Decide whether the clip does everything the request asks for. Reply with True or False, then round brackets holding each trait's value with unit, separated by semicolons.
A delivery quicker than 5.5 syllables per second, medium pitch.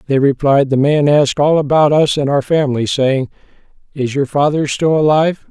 False (5.4 syllables/s; 145 Hz)